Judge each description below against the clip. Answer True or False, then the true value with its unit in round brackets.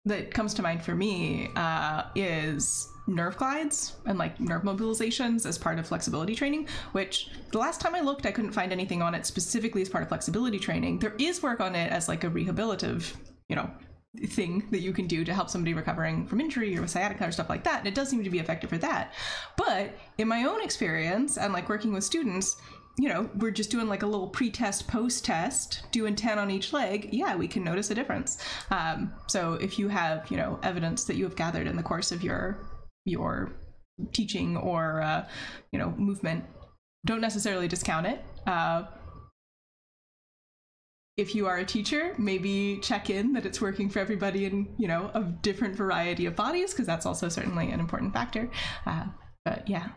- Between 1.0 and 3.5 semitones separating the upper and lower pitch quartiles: False (4.0 semitones)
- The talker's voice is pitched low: False (205 Hz)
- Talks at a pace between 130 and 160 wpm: False (200 wpm)